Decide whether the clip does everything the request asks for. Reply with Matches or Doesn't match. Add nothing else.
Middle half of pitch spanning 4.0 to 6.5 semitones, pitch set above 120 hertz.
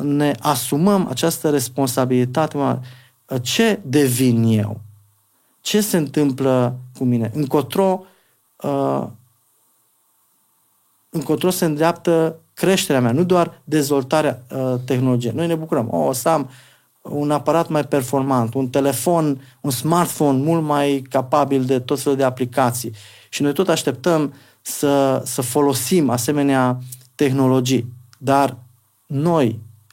Doesn't match